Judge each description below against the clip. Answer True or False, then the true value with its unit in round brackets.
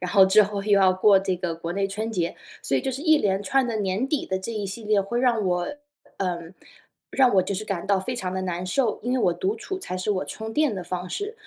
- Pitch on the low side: False (195 Hz)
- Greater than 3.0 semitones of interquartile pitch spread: True (3.4 semitones)